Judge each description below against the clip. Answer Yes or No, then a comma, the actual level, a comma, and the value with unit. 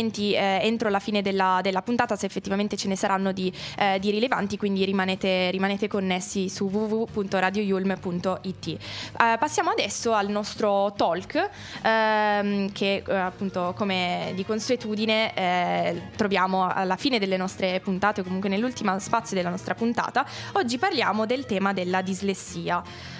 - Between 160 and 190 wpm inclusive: No, average, 140 wpm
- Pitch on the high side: Yes, high, 200 Hz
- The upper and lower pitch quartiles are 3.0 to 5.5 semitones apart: No, narrow, 2.4 semitones